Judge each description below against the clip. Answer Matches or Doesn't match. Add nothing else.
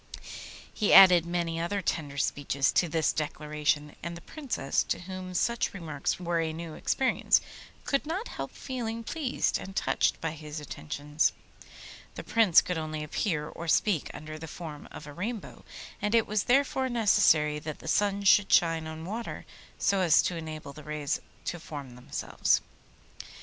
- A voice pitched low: Doesn't match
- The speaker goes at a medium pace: Matches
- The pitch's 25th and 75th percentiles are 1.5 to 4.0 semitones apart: Doesn't match